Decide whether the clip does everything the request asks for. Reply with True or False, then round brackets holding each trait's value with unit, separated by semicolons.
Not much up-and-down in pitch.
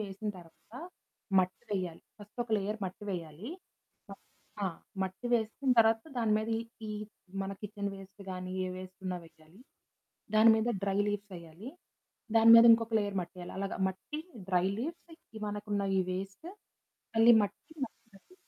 False (3.1 semitones)